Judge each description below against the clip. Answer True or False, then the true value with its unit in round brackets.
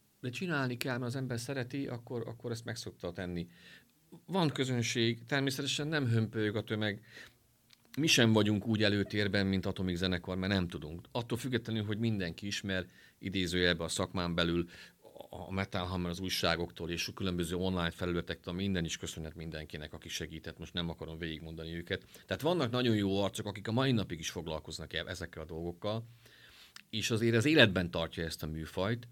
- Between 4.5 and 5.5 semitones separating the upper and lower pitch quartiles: True (5.2 semitones)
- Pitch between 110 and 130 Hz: False (95 Hz)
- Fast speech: True (170 wpm)